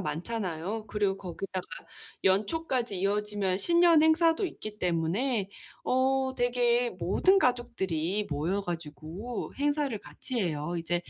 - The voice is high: Yes, high, 210 Hz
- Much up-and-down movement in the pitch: Yes, wide, 6.1 semitones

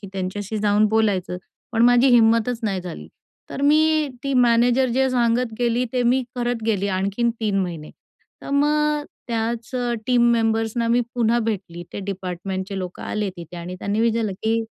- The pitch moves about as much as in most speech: Yes, average, 3.6 semitones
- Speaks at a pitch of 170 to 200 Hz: No, high, 225 Hz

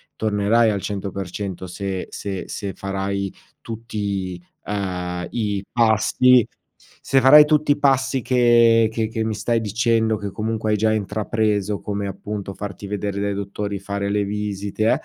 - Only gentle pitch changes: Yes, narrow, 2.3 semitones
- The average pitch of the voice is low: Yes, low, 105 Hz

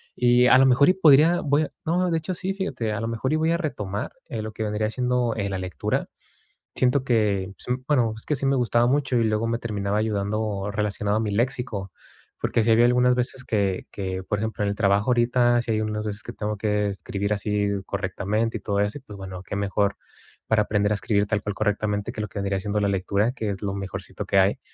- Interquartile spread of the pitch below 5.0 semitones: Yes, average, 3.4 semitones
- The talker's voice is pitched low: Yes, low, 110 Hz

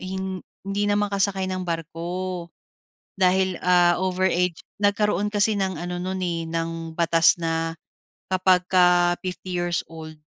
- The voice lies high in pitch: No, medium, 180 Hz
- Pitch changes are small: Yes, narrow, 1.9 semitones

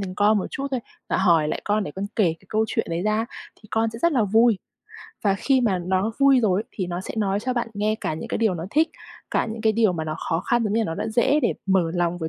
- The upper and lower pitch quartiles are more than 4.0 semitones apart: No, average, 3.7 semitones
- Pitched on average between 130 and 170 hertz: No, high, 210 Hz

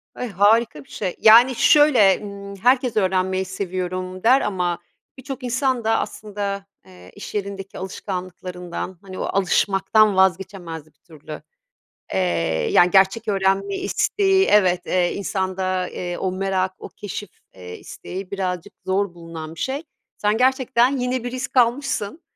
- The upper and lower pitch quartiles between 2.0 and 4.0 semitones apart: Yes, average, 3.6 semitones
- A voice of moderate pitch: No, high, 195 Hz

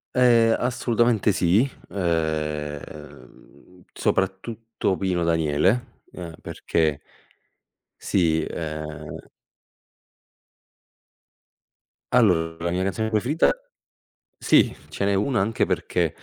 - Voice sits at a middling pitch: No, very low, 95 Hz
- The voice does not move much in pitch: No, wide, 5.8 semitones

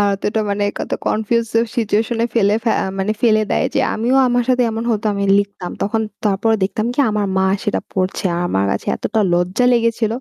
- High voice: Yes, high, 215 Hz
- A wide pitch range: No, narrow, 2.5 semitones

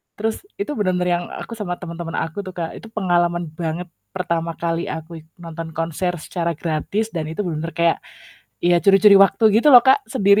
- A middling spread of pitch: Yes, average, 3.2 semitones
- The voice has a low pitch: No, medium, 175 Hz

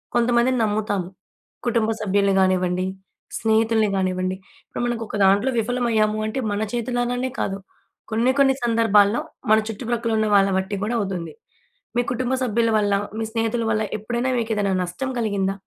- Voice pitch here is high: Yes, high, 220 Hz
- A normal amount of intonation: Yes, average, 3.0 semitones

